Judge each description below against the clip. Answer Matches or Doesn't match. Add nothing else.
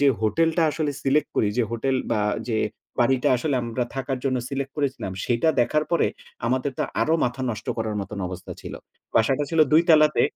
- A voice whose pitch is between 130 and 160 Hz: Matches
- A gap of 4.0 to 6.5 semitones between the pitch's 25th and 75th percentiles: Matches